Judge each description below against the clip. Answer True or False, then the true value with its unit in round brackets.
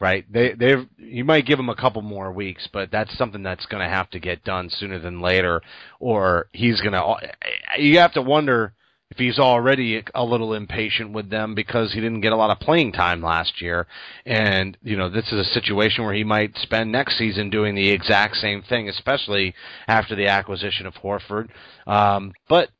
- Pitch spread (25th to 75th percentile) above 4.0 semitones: False (3.5 semitones)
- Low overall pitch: True (105 Hz)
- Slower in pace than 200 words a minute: False (205 wpm)